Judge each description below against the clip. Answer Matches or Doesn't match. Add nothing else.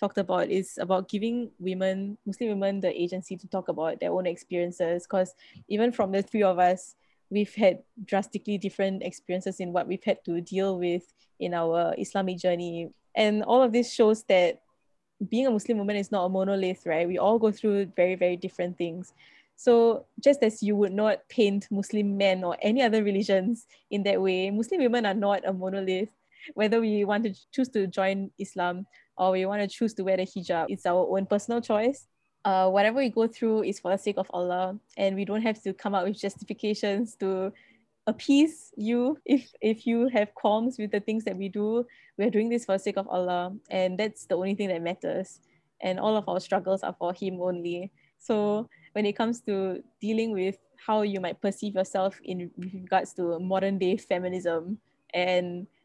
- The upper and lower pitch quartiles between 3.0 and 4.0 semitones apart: Doesn't match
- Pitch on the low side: Doesn't match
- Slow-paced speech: Doesn't match